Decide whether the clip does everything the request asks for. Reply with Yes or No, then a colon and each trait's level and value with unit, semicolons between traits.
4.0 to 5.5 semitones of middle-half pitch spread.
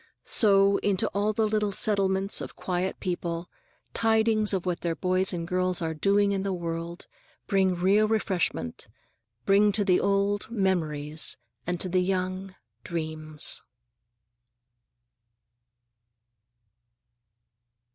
No: narrow, 2.5 semitones